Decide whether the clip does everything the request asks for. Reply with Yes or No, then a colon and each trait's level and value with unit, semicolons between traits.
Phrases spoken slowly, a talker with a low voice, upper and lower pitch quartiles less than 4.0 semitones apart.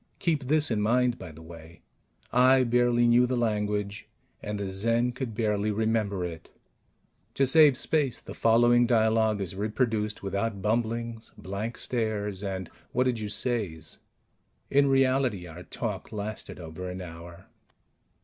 No: average, 145 wpm; low, 110 Hz; average, 3.6 semitones